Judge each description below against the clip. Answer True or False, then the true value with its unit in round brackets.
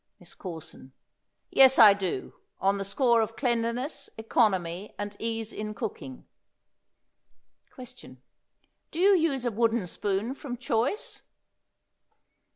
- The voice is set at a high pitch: True (225 Hz)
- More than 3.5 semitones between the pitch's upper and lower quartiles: True (4.2 semitones)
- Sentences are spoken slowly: True (115 wpm)